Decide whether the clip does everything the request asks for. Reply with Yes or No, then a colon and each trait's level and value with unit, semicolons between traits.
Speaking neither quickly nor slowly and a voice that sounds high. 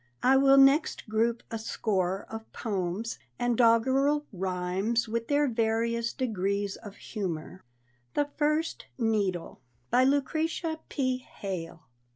No: slow, 120 wpm; high, 230 Hz